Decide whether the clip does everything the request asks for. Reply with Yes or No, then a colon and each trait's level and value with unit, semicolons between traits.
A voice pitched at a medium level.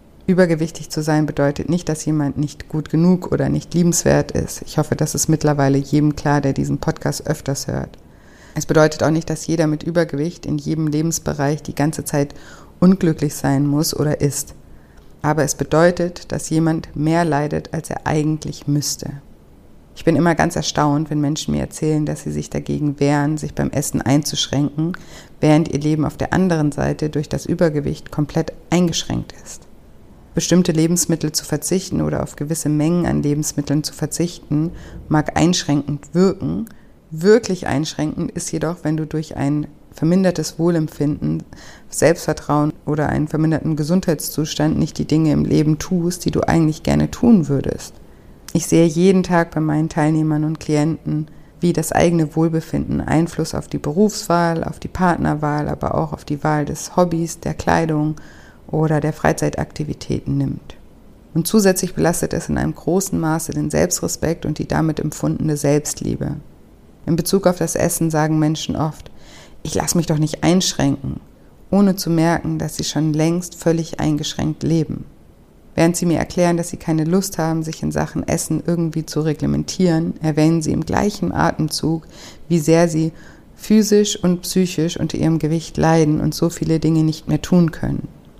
Yes: medium, 155 Hz